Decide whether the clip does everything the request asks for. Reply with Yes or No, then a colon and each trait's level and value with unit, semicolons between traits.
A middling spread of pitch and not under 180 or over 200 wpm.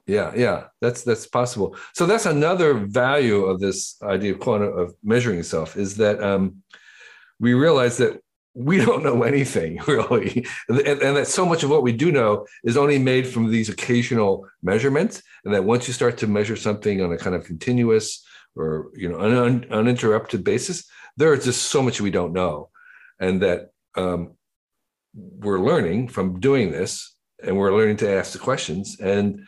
Yes: average, 4.0 semitones; average, 185 wpm